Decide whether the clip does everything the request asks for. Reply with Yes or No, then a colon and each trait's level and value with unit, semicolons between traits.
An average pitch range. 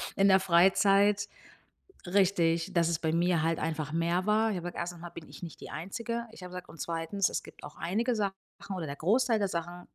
Yes: average, 3.2 semitones